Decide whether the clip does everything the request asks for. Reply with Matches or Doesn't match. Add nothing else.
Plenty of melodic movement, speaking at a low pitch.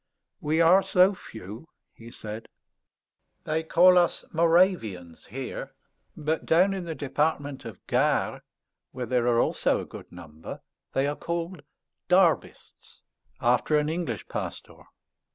Doesn't match